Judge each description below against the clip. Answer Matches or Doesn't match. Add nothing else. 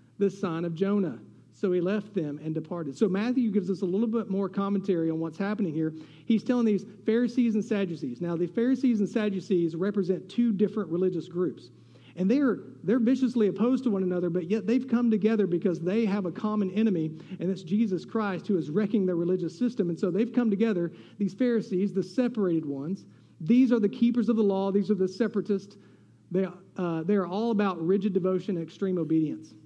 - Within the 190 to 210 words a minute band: Matches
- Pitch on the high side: Matches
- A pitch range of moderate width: Matches